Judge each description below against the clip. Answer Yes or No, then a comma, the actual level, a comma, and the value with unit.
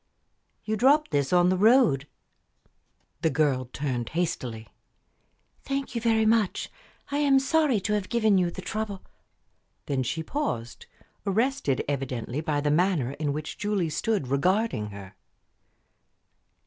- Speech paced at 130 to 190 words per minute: Yes, slow, 135 wpm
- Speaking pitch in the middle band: Yes, medium, 175 Hz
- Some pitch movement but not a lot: No, wide, 8.1 semitones